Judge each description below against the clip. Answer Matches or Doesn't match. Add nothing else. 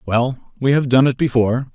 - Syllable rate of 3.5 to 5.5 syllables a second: Matches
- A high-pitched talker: Doesn't match